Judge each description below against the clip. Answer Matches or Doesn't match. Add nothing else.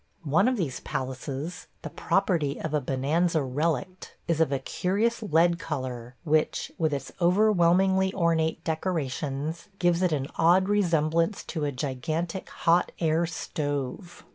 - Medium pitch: Matches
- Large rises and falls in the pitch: Doesn't match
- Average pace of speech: Matches